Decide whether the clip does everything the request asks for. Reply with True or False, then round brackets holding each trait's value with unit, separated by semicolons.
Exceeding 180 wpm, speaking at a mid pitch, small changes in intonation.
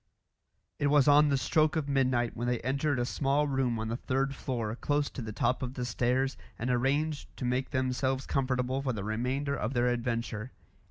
False (200 wpm; 130 Hz; 2.3 semitones)